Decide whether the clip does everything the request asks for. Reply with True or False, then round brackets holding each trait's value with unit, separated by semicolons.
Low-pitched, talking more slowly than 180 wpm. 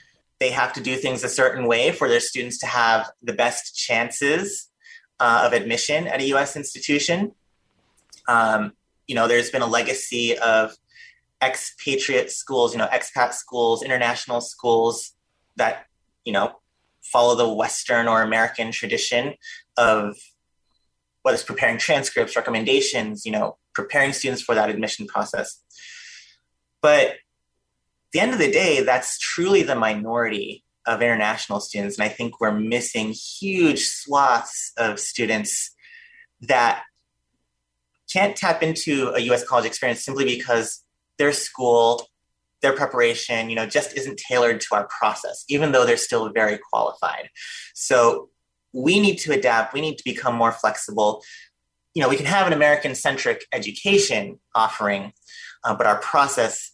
True (125 Hz; 145 wpm)